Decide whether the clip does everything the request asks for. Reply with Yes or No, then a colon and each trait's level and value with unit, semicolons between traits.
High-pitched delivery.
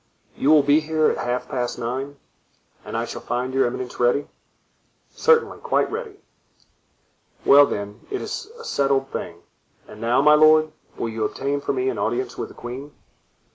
No: medium, 140 Hz